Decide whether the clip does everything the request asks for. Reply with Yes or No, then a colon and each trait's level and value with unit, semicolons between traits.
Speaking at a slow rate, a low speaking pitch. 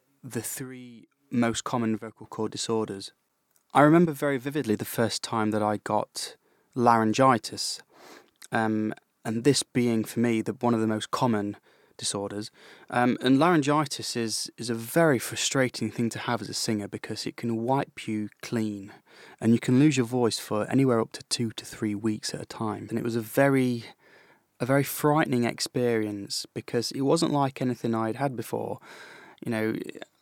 No: average, 175 wpm; low, 115 Hz